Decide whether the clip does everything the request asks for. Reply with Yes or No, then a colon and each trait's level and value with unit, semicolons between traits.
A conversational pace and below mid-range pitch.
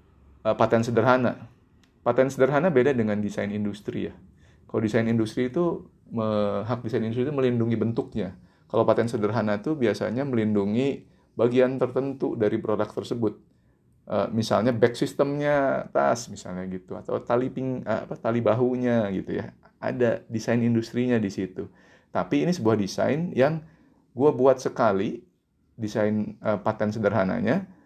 Yes: average, 130 wpm; low, 115 Hz